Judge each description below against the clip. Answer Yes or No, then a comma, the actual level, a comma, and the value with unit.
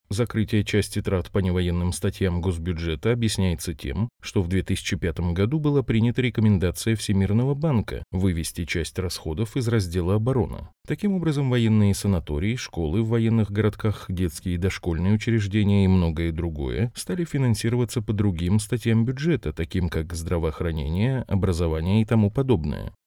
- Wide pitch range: No, average, 4.4 semitones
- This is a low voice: Yes, low, 100 Hz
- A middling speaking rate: Yes, average, 135 wpm